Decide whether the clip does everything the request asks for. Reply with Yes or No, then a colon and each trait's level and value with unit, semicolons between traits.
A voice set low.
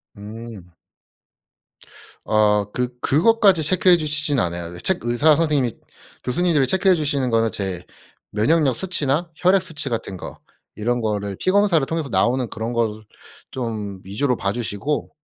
Yes: low, 125 Hz